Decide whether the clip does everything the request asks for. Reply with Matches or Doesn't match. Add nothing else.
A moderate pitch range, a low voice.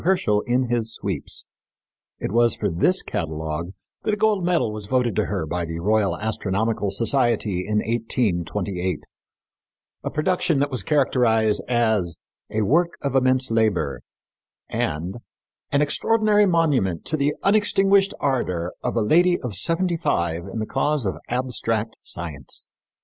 Doesn't match